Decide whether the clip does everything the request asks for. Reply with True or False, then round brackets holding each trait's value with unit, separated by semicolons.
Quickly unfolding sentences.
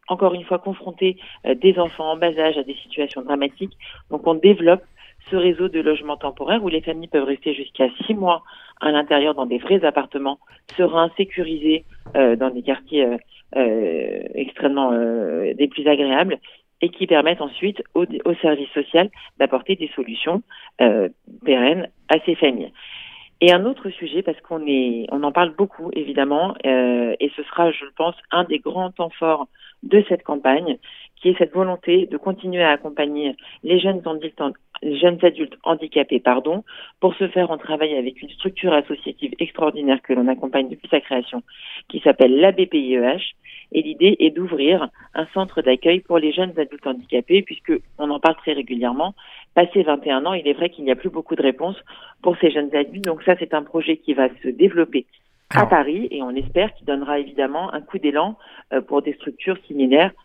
True (185 wpm)